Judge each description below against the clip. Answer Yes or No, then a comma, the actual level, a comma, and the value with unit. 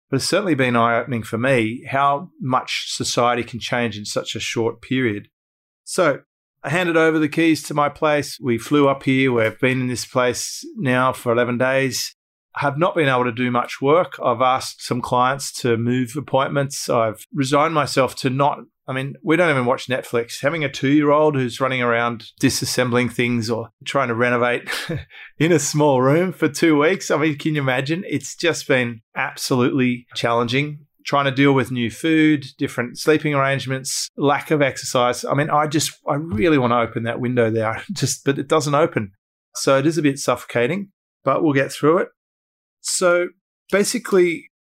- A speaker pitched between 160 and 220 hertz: No, low, 135 Hz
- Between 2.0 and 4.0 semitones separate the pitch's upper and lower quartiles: Yes, average, 3.5 semitones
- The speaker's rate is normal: Yes, average, 190 wpm